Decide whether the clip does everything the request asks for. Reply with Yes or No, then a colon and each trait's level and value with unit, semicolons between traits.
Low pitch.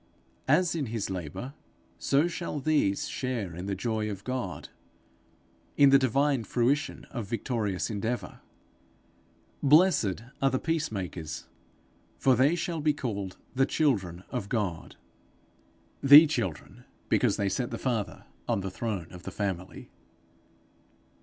Yes: low, 120 Hz